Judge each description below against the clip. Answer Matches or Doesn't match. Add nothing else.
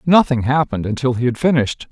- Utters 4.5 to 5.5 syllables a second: Doesn't match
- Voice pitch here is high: Doesn't match